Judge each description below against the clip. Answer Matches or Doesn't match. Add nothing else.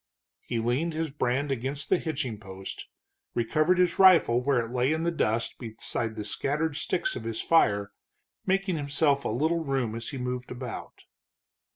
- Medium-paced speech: Matches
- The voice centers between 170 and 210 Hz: Doesn't match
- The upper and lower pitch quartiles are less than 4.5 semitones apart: Doesn't match